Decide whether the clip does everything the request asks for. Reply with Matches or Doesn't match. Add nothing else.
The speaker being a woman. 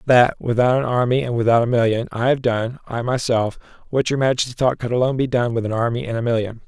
Doesn't match